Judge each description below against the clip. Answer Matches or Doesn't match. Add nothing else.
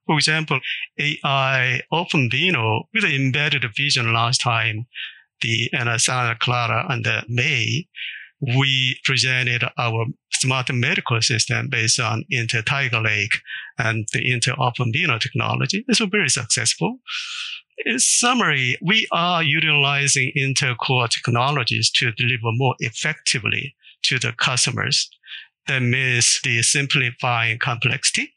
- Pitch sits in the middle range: Doesn't match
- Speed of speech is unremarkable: Doesn't match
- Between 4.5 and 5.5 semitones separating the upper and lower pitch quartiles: Doesn't match